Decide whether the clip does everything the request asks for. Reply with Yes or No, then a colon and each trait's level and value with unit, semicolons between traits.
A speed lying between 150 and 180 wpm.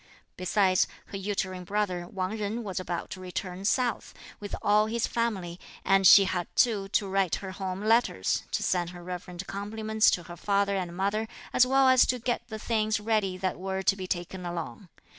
No: average, 190 wpm